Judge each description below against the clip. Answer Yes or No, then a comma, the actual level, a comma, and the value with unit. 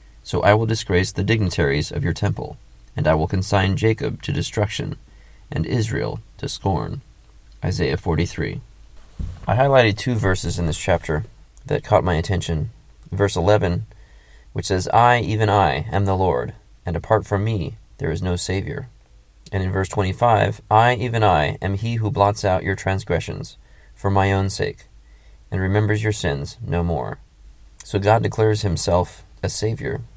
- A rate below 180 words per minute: Yes, average, 160 wpm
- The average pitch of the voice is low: Yes, very low, 95 Hz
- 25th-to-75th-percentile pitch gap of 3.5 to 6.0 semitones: Yes, average, 4.2 semitones